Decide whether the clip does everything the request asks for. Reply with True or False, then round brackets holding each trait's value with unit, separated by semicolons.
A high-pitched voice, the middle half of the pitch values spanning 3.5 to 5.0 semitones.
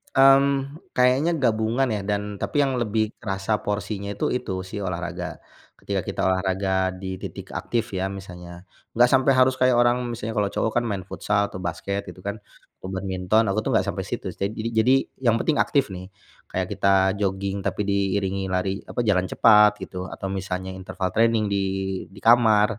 False (105 Hz; 3.9 semitones)